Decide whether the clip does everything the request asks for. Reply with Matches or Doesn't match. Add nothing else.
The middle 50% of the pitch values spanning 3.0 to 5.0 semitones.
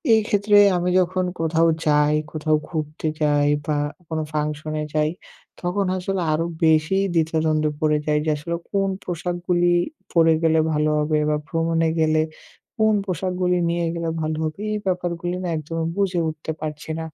Doesn't match